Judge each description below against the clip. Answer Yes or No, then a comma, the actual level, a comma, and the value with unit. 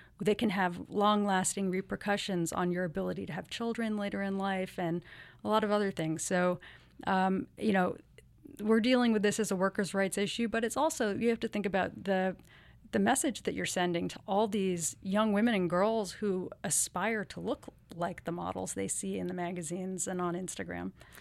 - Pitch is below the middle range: No, high, 195 Hz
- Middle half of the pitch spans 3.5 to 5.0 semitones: No, average, 2.8 semitones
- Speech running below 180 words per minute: No, average, 195 wpm